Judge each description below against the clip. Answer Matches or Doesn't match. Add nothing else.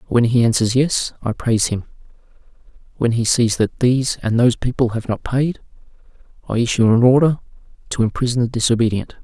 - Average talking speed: Matches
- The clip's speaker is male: Matches